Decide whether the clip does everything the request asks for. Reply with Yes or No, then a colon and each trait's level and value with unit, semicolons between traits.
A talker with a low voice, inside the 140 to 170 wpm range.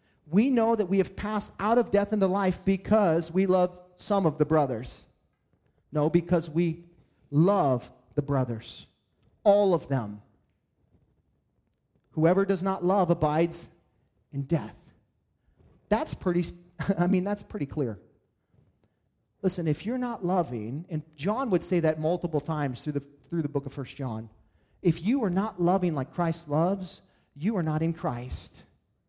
No: medium, 170 Hz; average, 155 wpm